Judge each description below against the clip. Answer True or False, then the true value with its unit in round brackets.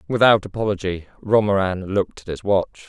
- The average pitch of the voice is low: True (100 Hz)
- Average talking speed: True (145 wpm)